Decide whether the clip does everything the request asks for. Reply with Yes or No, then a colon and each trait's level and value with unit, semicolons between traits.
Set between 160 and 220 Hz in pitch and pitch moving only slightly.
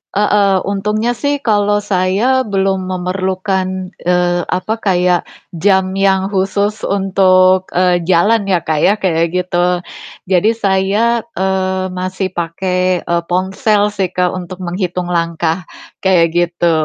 Yes: medium, 185 Hz; narrow, 1.7 semitones